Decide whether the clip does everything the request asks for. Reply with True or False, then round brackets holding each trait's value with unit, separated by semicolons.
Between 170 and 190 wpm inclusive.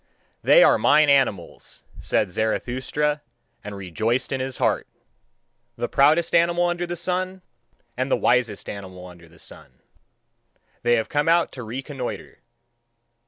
False (135 wpm)